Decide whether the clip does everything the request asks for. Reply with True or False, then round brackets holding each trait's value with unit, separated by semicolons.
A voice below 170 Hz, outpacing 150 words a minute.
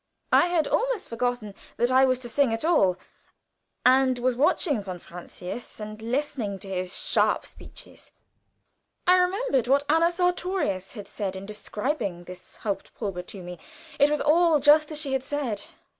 False (255 Hz; 165 wpm)